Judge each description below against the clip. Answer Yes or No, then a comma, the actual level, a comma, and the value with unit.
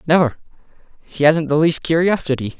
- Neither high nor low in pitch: Yes, medium, 155 Hz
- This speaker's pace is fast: No, average, 140 wpm